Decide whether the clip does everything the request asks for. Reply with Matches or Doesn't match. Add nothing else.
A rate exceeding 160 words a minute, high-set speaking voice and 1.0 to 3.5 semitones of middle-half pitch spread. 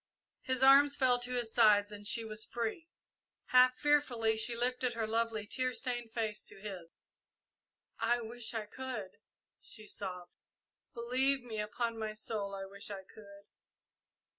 Doesn't match